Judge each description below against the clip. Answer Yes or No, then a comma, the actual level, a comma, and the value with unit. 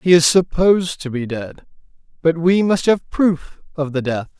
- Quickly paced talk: No, average, 190 wpm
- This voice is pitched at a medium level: Yes, medium, 160 Hz